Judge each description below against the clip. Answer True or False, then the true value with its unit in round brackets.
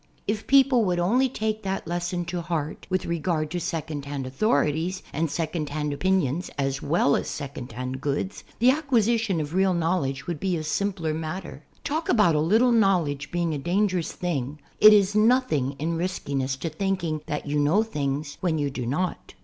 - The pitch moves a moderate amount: True (4.9 semitones)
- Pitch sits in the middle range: True (170 Hz)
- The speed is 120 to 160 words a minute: False (180 wpm)